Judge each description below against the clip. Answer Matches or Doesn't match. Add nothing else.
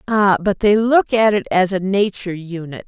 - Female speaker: Matches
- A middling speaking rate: Doesn't match